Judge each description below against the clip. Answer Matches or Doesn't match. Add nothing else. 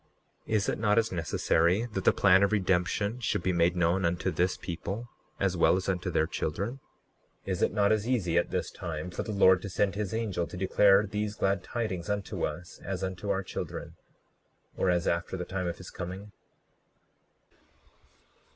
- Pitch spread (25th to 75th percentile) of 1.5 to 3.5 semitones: Matches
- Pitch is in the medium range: Doesn't match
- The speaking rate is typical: Matches